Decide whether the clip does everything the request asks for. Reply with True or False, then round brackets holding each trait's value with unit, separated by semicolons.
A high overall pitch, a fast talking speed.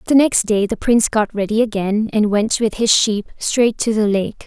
True (215 Hz; 230 wpm)